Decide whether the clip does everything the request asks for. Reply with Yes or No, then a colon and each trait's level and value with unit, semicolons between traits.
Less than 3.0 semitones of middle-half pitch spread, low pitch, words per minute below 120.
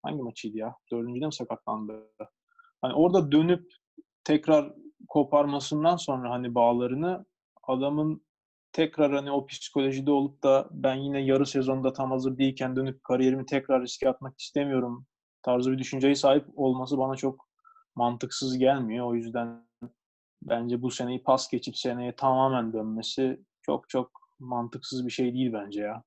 No: narrow, 2.4 semitones; low, 130 Hz; fast, 140 wpm